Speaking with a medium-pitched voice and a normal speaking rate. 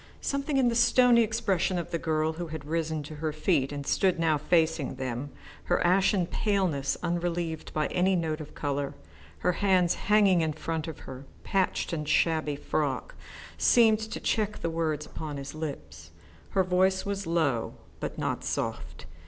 Yes: medium, 165 Hz; average, 170 wpm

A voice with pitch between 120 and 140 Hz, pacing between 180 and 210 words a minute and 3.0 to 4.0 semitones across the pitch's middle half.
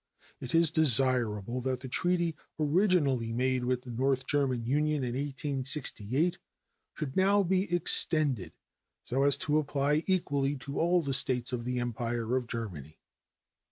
No: low, 135 Hz; average, 145 wpm; average, 3.7 semitones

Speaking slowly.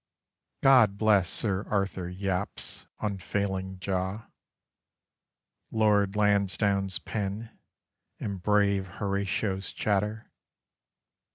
Yes: slow, 75 wpm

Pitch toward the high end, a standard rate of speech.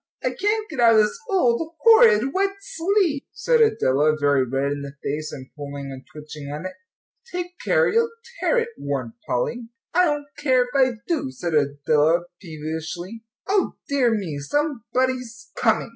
Yes: high, 225 Hz; average, 165 wpm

